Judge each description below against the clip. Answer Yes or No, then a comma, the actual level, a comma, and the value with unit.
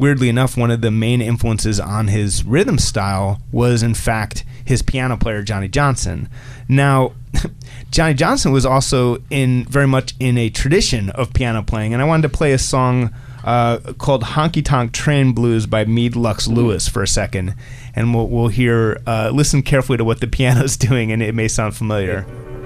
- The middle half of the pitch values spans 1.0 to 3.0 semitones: Yes, average, 2.7 semitones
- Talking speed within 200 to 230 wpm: No, average, 185 wpm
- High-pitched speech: No, low, 120 Hz